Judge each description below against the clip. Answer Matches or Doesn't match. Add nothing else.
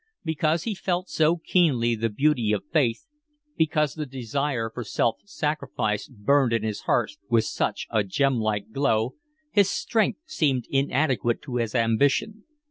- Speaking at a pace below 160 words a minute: Matches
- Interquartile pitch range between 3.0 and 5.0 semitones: Doesn't match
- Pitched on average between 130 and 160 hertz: Matches